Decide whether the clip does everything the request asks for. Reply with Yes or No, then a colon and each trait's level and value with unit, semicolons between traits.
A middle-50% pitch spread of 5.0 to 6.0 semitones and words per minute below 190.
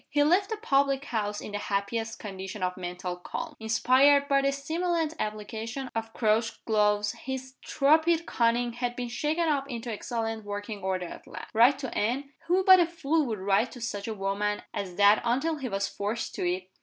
No: average, 5.3 semitones; average, 195 wpm